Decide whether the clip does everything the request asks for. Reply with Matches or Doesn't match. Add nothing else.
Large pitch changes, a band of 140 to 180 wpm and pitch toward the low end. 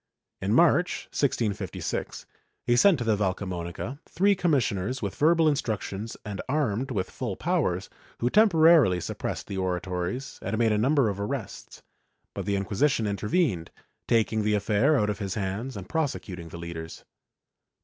Matches